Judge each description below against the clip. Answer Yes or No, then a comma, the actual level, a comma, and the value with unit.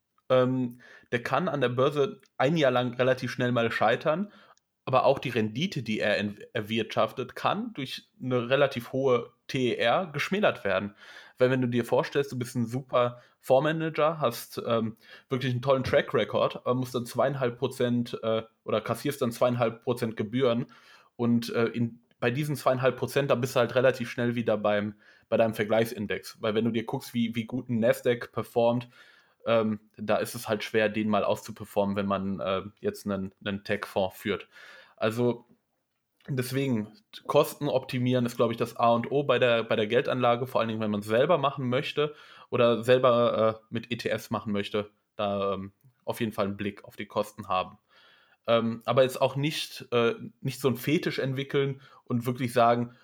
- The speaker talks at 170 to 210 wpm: Yes, average, 180 wpm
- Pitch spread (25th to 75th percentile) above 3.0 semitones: No, average, 2.7 semitones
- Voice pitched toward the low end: Yes, low, 120 Hz